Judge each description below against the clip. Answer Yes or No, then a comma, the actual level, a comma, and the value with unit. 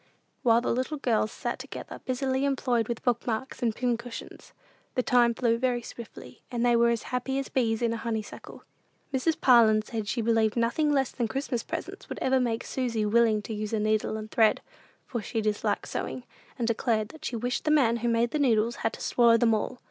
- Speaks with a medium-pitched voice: No, high, 235 Hz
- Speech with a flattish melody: Yes, narrow, 2.0 semitones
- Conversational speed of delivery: No, fast, 210 wpm